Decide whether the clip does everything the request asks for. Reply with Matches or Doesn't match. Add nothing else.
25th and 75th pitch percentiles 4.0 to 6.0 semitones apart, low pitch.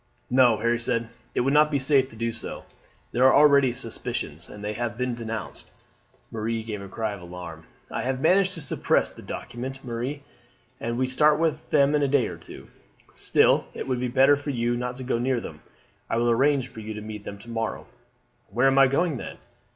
Doesn't match